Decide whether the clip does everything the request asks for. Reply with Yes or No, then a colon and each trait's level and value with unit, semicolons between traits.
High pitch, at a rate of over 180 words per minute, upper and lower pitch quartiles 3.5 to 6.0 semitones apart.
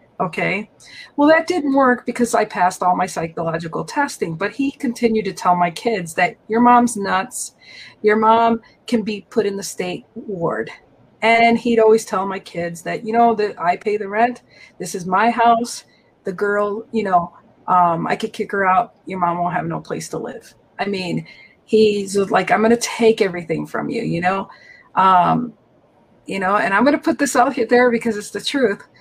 Yes: high, 215 Hz; average, 200 wpm; average, 4.0 semitones